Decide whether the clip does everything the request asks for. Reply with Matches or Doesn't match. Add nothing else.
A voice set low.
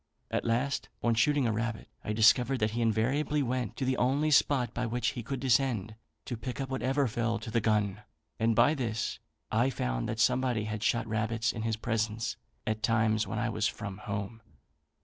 Matches